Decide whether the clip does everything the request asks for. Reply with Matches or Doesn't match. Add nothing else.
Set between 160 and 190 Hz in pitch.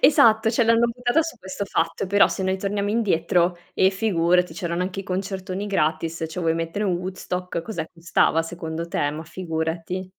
Matches